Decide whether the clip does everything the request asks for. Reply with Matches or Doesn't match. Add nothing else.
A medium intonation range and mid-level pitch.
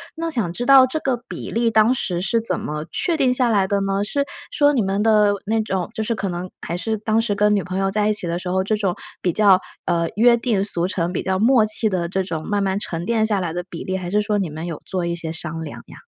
Doesn't match